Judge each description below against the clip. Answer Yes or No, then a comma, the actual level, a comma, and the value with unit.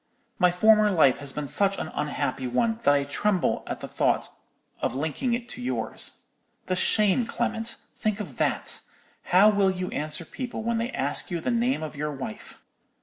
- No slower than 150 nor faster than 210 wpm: Yes, average, 180 wpm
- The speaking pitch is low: No, medium, 185 Hz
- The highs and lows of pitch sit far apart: Yes, wide, 7.5 semitones